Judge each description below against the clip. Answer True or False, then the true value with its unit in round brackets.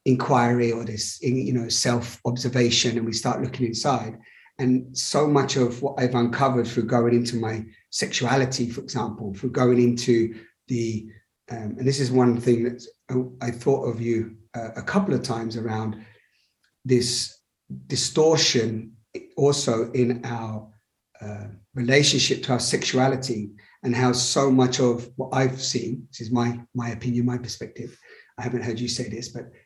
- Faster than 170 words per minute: False (160 wpm)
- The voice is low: True (120 Hz)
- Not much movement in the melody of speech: True (1.8 semitones)